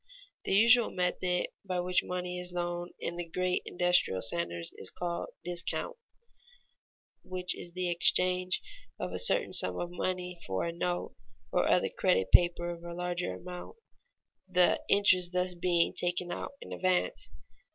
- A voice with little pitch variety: Yes, narrow, 0.8 semitones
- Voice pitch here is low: No, medium, 180 Hz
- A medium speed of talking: Yes, average, 150 wpm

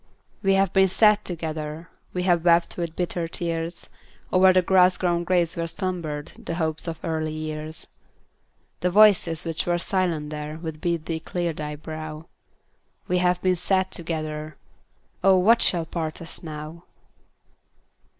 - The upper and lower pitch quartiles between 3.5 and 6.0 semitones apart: No, narrow, 2.4 semitones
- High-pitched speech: No, medium, 170 Hz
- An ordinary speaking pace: Yes, average, 150 wpm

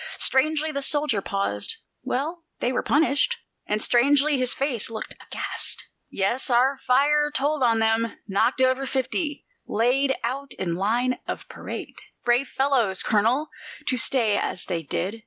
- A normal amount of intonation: Yes, average, 3.9 semitones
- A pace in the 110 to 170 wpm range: Yes, average, 145 wpm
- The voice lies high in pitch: Yes, very high, 255 Hz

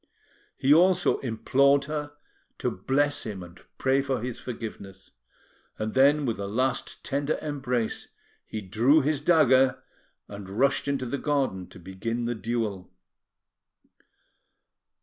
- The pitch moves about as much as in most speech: Yes, average, 4.6 semitones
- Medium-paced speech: No, slow, 130 wpm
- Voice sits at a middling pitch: No, low, 130 Hz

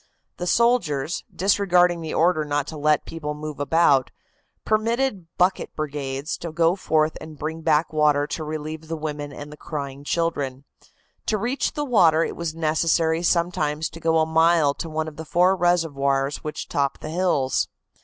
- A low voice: No, medium, 160 Hz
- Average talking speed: Yes, average, 170 wpm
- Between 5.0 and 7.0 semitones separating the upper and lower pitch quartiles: No, narrow, 2.5 semitones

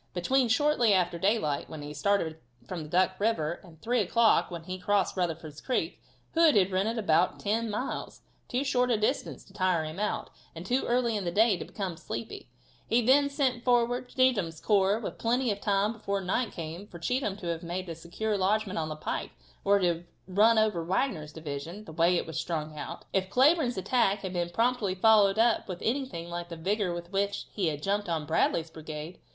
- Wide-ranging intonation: No, average, 5.0 semitones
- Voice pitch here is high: Yes, high, 195 Hz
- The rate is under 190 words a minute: No, fast, 205 wpm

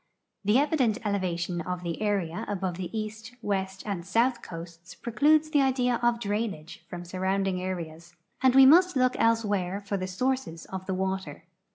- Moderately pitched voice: No, high, 200 Hz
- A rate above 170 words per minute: No, average, 165 wpm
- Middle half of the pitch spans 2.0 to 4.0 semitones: No, average, 4.7 semitones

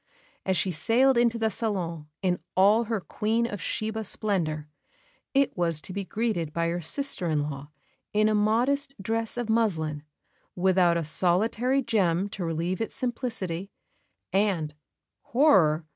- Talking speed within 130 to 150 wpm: Yes, average, 145 wpm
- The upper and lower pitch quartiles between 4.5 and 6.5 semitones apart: Yes, average, 5.1 semitones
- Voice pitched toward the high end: Yes, high, 195 Hz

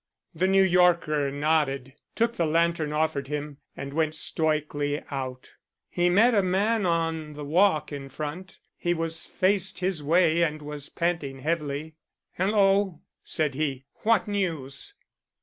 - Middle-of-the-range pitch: Yes, medium, 160 Hz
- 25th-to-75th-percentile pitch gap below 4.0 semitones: Yes, average, 3.6 semitones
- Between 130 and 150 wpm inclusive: Yes, average, 140 wpm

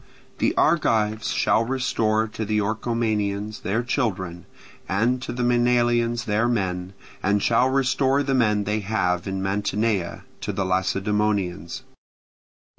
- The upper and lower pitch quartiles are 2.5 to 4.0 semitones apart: Yes, average, 3.2 semitones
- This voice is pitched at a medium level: No, low, 110 Hz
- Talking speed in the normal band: No, slow, 125 wpm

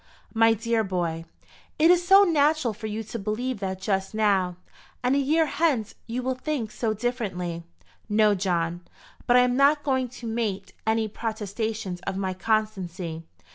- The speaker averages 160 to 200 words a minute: Yes, average, 165 wpm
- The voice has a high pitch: Yes, high, 220 Hz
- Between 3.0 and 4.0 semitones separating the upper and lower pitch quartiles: No, average, 4.6 semitones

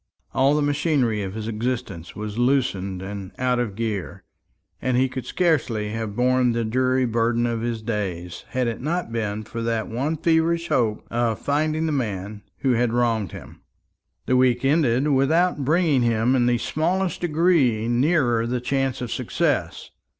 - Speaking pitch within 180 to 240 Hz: No, low, 120 Hz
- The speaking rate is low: No, average, 165 wpm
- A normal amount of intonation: Yes, average, 3.9 semitones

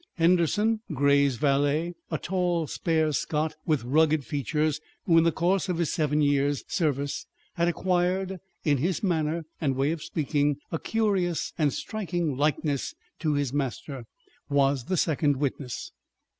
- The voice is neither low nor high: Yes, medium, 155 Hz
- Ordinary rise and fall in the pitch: Yes, average, 3.5 semitones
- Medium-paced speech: Yes, average, 145 wpm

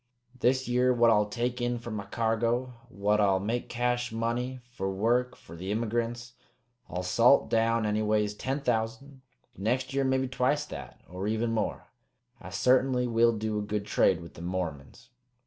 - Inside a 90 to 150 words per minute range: No, average, 165 wpm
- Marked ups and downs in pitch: No, average, 3.0 semitones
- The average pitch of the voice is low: Yes, low, 115 Hz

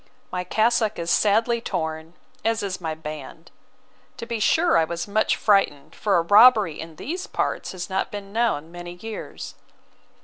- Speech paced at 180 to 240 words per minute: No, average, 165 wpm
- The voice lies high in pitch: Yes, high, 195 Hz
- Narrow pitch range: No, average, 5.0 semitones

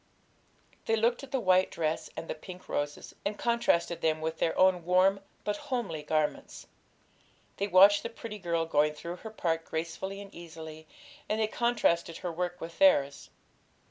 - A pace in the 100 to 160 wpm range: No, average, 170 wpm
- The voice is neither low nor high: Yes, medium, 180 Hz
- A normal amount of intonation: Yes, average, 4.5 semitones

